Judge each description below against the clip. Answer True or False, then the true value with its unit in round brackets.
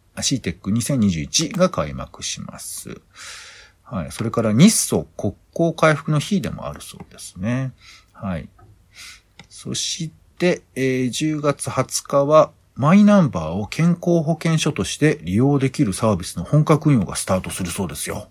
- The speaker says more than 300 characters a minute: False (275 characters per minute)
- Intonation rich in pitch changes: True (7.6 semitones)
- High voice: False (140 Hz)